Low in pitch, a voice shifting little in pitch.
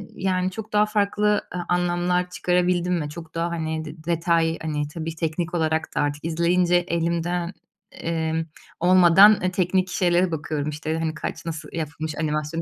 No: medium, 170 Hz; narrow, 2.1 semitones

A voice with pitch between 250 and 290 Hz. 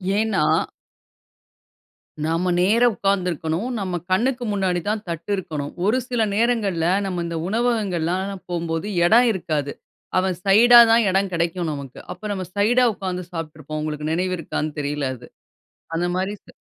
No: medium, 185 Hz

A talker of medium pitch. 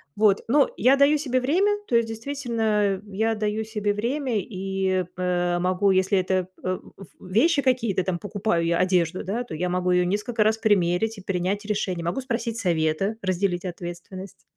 No: high, 200 Hz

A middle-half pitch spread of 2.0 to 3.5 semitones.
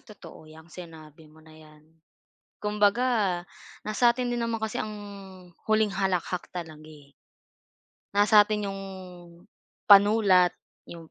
No: average, 5.0 semitones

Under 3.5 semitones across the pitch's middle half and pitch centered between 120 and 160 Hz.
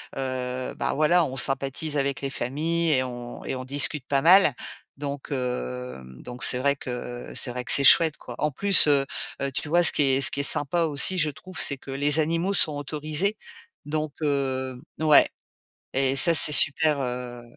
Yes: average, 3.1 semitones; medium, 140 Hz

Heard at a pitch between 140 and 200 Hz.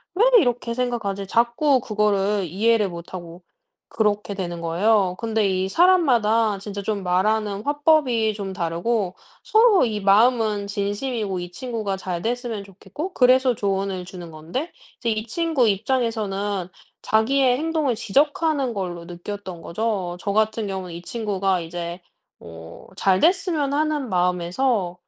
No: high, 210 Hz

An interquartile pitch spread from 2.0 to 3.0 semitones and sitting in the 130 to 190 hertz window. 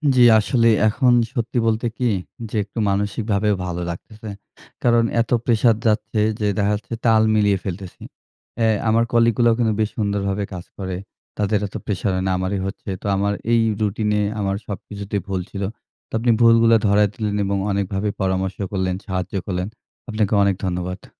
No: narrow, 2.4 semitones; low, 105 Hz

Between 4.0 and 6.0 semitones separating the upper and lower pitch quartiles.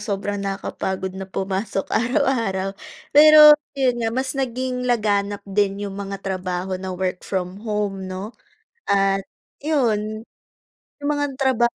Yes: average, 4.4 semitones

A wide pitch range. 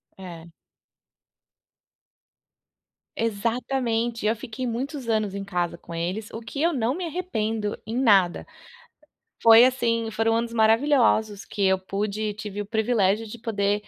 No: average, 2.7 semitones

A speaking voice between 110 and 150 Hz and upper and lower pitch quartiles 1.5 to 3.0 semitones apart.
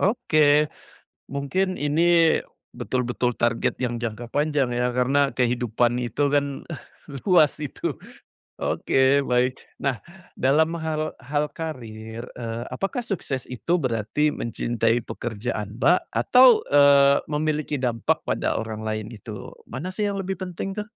No: medium, 140 Hz; average, 4.7 semitones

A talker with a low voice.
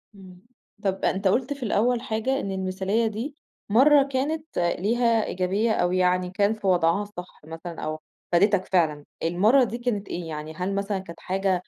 No: high, 195 Hz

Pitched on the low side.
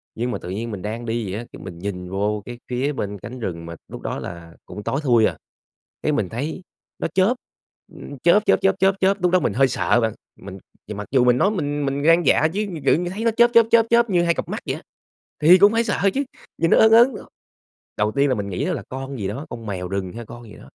Yes: low, 130 Hz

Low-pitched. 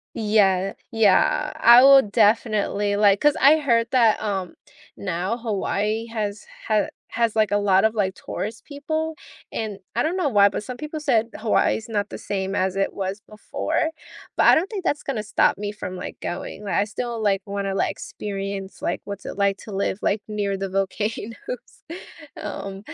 No: high, 210 Hz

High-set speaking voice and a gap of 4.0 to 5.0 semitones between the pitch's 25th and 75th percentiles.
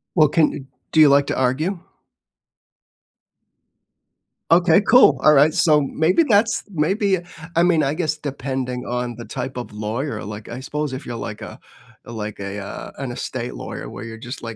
No: medium, 140 Hz; average, 4.6 semitones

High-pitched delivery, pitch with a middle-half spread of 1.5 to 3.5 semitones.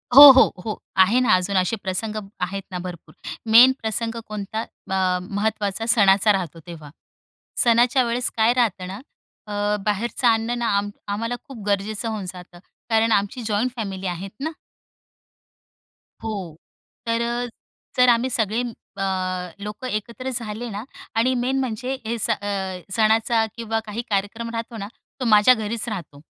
Yes: high, 220 Hz; average, 2.9 semitones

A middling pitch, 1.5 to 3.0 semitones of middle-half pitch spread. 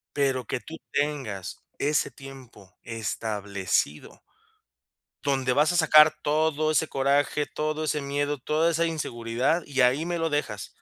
No: medium, 145 Hz; average, 3.9 semitones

